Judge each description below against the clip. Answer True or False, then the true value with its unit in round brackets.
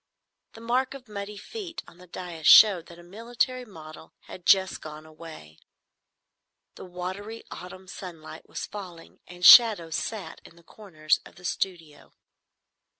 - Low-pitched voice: False (180 Hz)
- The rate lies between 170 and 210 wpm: False (150 wpm)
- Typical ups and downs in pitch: True (4.4 semitones)